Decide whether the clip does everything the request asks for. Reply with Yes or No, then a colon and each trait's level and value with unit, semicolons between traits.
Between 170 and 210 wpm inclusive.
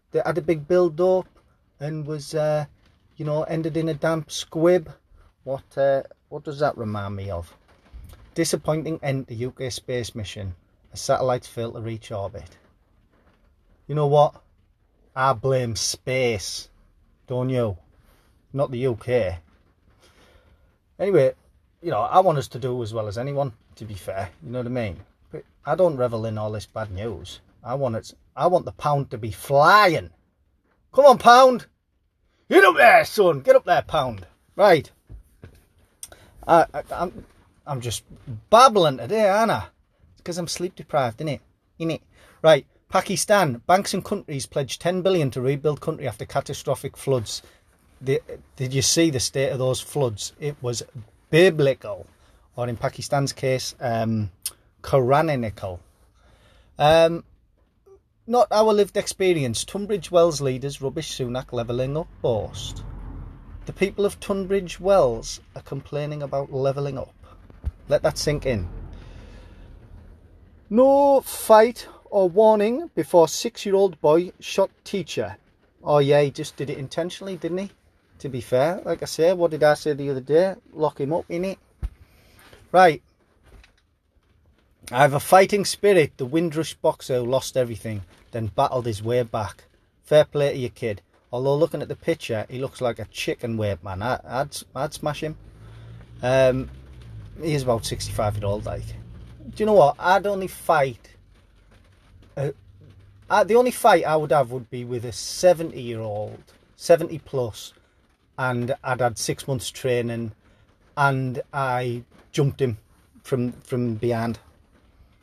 No: average, 150 wpm